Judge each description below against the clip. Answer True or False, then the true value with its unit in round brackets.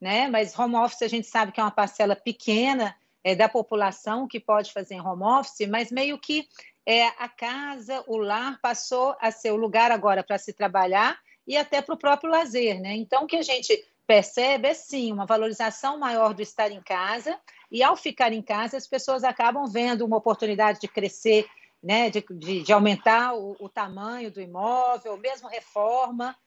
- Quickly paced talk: True (195 wpm)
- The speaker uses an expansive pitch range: False (3.5 semitones)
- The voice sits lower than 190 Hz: False (225 Hz)